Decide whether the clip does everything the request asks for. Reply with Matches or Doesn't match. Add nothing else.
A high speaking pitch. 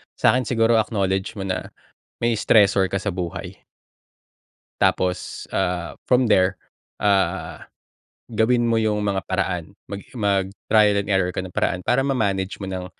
Doesn't match